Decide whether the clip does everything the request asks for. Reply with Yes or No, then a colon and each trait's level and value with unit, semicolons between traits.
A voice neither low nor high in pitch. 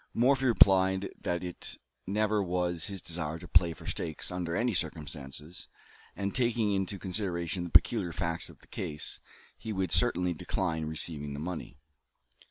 No: very low, 90 Hz